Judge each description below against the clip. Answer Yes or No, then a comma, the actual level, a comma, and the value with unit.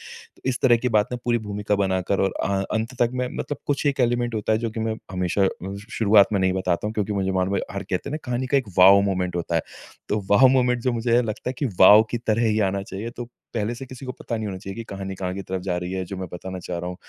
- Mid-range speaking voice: No, low, 105 Hz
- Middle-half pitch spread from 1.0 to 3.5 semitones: No, average, 4.0 semitones